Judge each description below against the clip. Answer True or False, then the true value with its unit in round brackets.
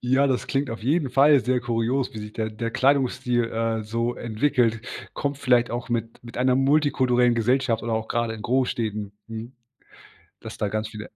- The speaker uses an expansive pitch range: False (2.7 semitones)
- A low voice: True (120 Hz)